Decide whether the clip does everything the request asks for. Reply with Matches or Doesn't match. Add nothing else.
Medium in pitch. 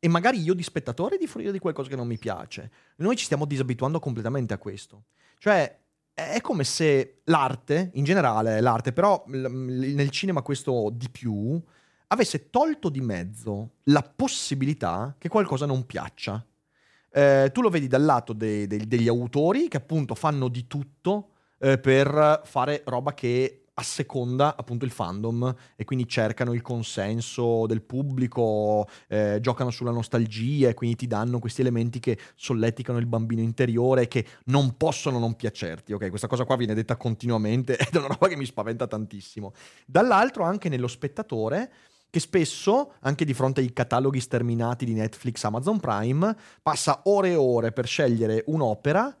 Doesn't match